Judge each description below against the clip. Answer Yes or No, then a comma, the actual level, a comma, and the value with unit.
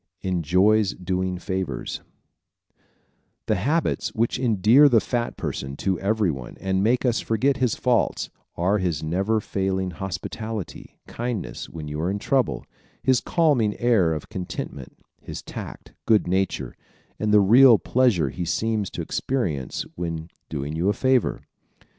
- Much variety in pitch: No, average, 4.6 semitones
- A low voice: Yes, low, 100 Hz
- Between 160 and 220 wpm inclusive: No, average, 140 wpm